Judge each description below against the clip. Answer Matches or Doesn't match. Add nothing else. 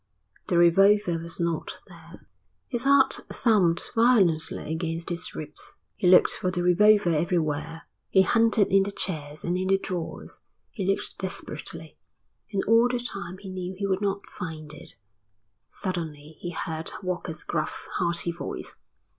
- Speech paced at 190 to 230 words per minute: Doesn't match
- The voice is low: Doesn't match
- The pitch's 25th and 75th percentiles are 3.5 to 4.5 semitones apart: Doesn't match